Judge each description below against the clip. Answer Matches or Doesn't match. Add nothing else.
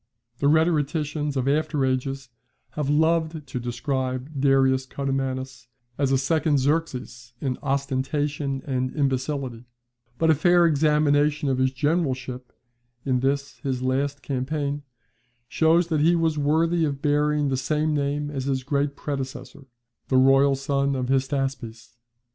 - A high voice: Doesn't match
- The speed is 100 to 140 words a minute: Matches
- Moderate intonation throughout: Doesn't match